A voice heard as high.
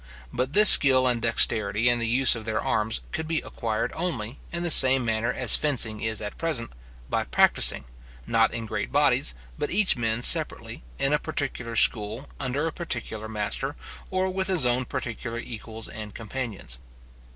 No: low, 120 Hz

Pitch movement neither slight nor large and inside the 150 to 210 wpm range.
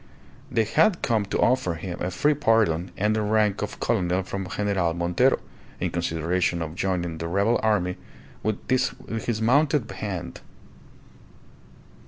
No: average, 4.2 semitones; average, 140 wpm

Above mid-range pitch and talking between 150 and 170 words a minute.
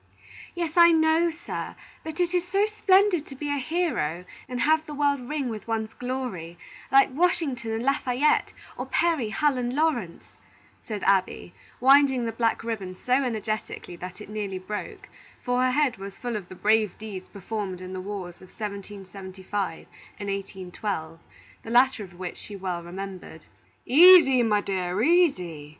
Yes: high, 225 Hz; average, 165 wpm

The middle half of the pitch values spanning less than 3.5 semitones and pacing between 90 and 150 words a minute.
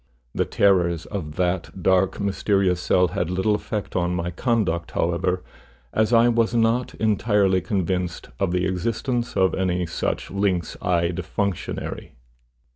Yes: average, 2.8 semitones; slow, 135 wpm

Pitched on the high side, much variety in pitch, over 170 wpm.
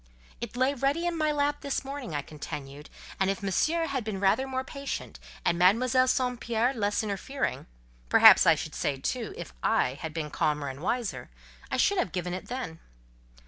Yes: high, 230 Hz; wide, 8.7 semitones; average, 180 wpm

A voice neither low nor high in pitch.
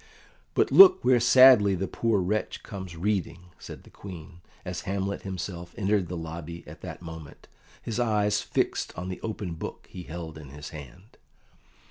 No: very low, 95 Hz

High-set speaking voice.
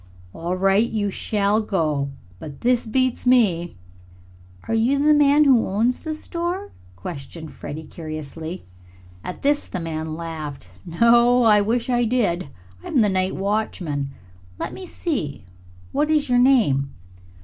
Yes: high, 205 Hz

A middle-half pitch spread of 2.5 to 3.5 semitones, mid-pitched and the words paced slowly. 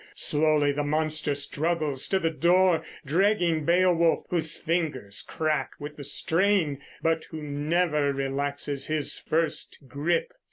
Yes: average, 2.8 semitones; medium, 155 Hz; slow, 125 wpm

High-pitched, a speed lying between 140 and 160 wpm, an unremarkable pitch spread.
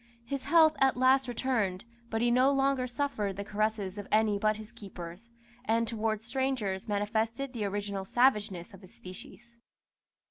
Yes: high, 220 Hz; average, 155 wpm; average, 4.0 semitones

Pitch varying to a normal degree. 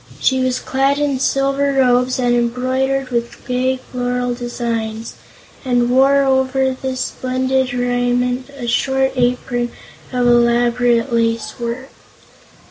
No: narrow, 1.5 semitones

